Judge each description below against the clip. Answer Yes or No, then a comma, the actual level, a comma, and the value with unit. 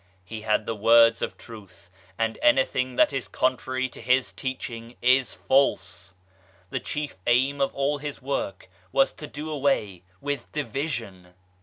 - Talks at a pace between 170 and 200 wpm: No, average, 150 wpm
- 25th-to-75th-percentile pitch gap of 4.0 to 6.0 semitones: No, average, 3.4 semitones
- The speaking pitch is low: Yes, low, 130 Hz